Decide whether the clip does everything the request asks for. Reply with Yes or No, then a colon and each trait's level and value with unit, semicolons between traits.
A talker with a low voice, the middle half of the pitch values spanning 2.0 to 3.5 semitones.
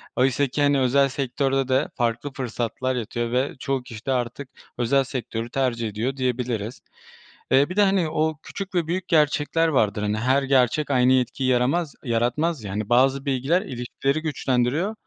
Yes: low, 130 Hz; average, 2.9 semitones